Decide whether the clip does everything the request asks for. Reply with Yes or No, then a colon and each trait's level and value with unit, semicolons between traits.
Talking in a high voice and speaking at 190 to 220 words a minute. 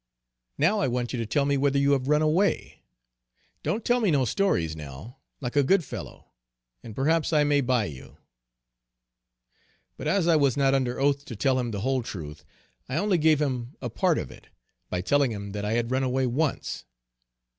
No: low, 135 Hz; average, 200 wpm